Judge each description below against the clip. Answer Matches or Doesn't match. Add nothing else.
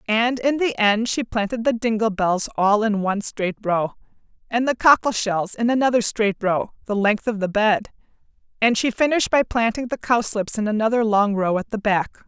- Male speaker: Doesn't match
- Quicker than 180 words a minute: Matches